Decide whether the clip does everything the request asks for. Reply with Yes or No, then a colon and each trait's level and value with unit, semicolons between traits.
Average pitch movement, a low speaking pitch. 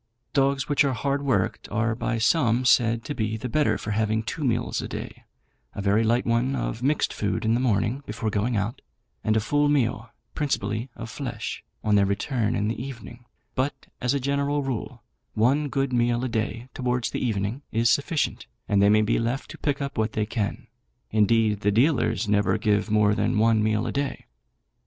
Yes: average, 3.7 semitones; low, 115 Hz